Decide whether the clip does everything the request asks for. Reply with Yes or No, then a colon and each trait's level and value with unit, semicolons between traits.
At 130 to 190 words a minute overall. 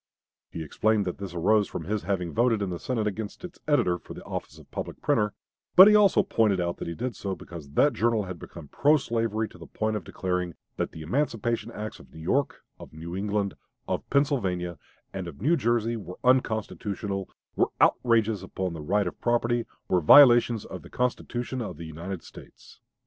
No: average, 200 wpm